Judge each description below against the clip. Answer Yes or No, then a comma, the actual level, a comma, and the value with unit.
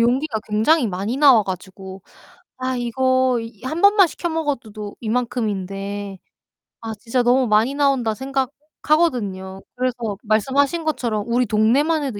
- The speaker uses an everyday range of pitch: Yes, average, 4.4 semitones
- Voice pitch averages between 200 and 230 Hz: No, high, 240 Hz